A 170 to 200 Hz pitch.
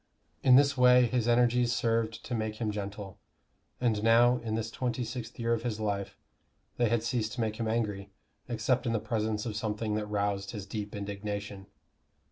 No: low, 110 Hz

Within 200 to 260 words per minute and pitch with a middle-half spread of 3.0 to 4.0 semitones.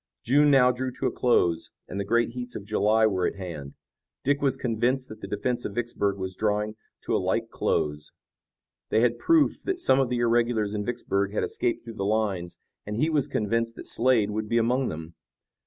Yes: fast, 205 wpm; average, 3.5 semitones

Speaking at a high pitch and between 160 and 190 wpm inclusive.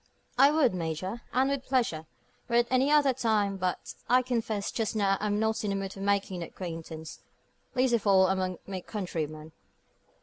Yes: high, 200 Hz; average, 180 wpm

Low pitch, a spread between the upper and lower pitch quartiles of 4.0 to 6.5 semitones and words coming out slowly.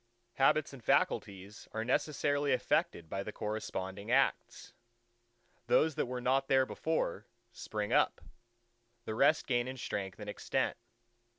Yes: low, 120 Hz; average, 4.7 semitones; slow, 130 wpm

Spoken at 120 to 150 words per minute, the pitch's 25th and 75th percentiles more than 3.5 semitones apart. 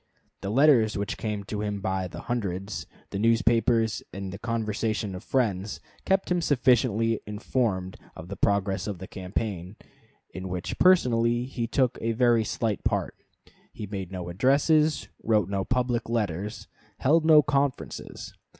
Yes: average, 145 wpm; average, 3.9 semitones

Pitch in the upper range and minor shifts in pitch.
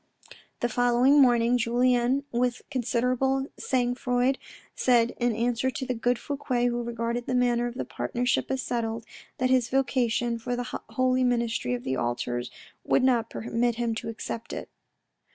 Yes: high, 245 Hz; narrow, 1.5 semitones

